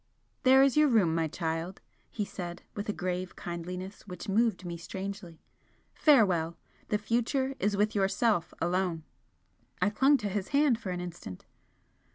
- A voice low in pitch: No, high, 195 Hz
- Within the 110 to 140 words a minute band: No, average, 155 wpm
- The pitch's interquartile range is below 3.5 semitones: No, average, 4.2 semitones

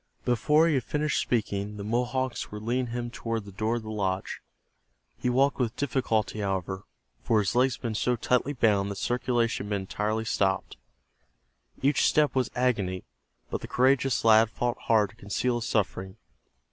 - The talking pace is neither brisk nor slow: Yes, average, 175 wpm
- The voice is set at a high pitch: No, low, 115 Hz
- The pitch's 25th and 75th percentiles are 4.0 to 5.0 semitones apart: No, average, 3.3 semitones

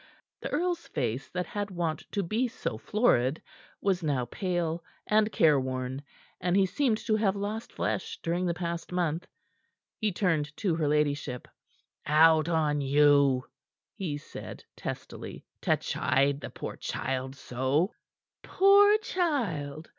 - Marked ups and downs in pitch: Yes, wide, 6.0 semitones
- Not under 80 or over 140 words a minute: Yes, slow, 135 wpm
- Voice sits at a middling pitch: Yes, medium, 165 Hz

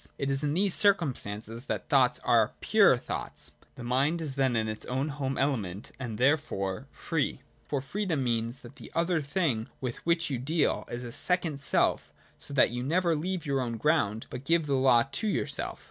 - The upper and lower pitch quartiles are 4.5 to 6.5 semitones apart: Yes, average, 5.2 semitones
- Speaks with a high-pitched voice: No, low, 135 Hz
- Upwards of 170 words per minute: Yes, average, 200 wpm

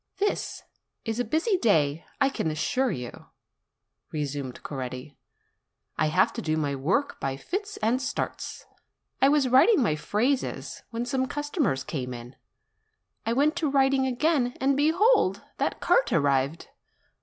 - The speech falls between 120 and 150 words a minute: Yes, average, 145 wpm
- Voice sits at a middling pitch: No, high, 240 Hz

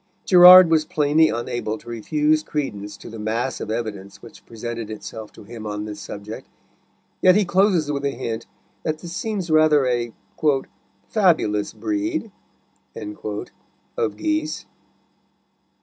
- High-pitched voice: No, low, 135 Hz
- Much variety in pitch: Yes, wide, 8.1 semitones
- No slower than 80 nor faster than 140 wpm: Yes, slow, 135 wpm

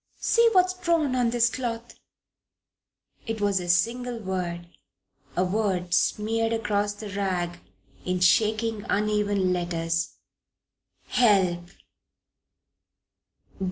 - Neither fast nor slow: No, slow, 100 wpm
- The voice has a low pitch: No, high, 205 Hz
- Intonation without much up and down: No, average, 4.1 semitones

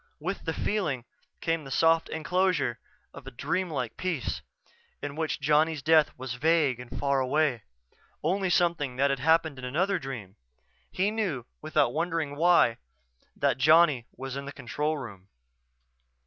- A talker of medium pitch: Yes, medium, 150 Hz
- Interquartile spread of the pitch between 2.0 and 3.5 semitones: No, average, 3.9 semitones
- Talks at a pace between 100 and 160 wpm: Yes, average, 150 wpm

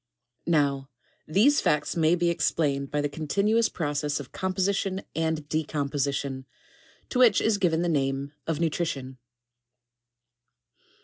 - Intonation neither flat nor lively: Yes, average, 3.9 semitones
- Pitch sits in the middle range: Yes, medium, 155 Hz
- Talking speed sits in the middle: No, slow, 125 wpm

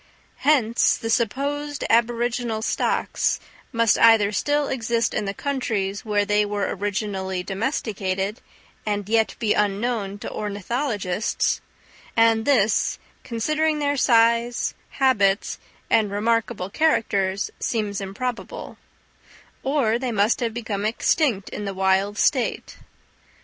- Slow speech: Yes, slow, 115 wpm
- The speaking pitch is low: No, high, 225 Hz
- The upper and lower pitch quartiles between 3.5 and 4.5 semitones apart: No, average, 3.1 semitones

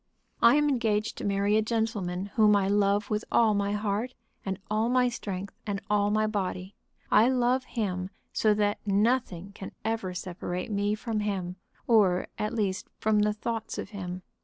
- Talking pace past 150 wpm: Yes, average, 175 wpm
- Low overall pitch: No, high, 210 Hz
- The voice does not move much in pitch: Yes, narrow, 2.2 semitones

